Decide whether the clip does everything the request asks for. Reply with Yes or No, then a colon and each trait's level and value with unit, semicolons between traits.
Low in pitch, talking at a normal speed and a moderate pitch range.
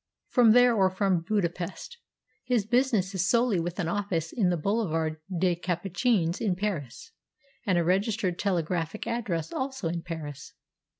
No: medium, 185 Hz; average, 145 wpm; average, 4.4 semitones